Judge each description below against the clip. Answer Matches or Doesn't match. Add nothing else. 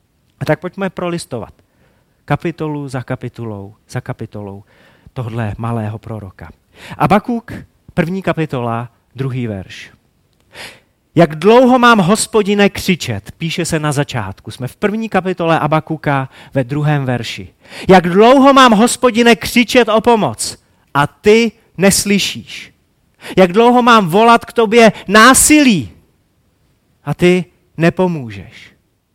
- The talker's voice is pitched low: Doesn't match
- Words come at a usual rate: Doesn't match